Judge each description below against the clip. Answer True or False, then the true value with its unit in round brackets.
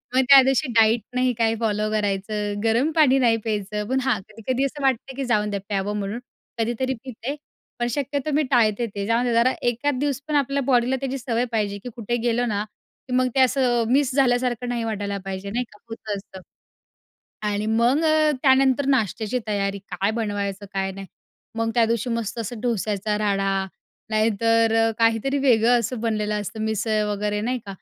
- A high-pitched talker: True (230 Hz)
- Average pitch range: True (3.4 semitones)